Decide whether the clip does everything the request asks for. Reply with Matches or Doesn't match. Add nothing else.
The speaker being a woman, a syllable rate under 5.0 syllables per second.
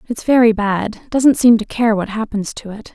Matches